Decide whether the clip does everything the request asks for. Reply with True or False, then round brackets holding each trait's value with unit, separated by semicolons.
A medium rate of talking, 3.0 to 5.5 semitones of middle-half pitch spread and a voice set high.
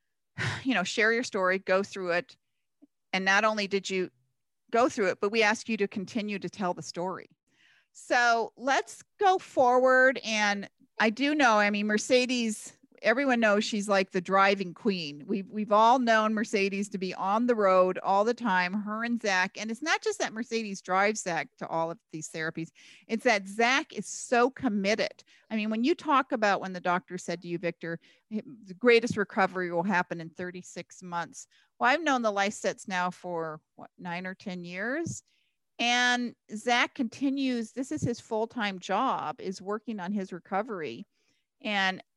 True (180 wpm; 4.3 semitones; 210 Hz)